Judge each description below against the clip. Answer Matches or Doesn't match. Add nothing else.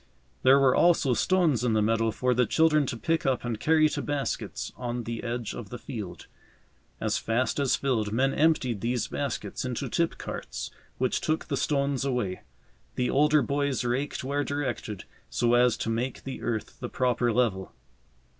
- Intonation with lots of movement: Doesn't match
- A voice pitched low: Matches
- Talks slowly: Doesn't match